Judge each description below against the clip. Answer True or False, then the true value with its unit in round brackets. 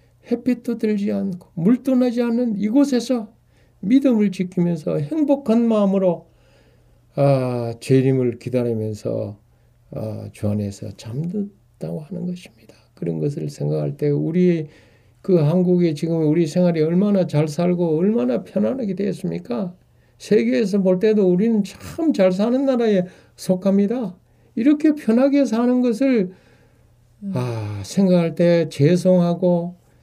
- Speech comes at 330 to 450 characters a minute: False (270 characters per minute)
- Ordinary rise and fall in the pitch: False (8.4 semitones)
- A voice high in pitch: False (180 Hz)